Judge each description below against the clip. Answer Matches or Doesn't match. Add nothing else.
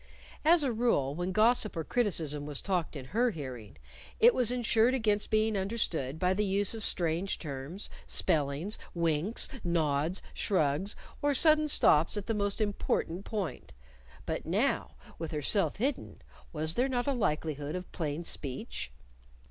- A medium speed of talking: Matches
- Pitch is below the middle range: Doesn't match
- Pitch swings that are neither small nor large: Doesn't match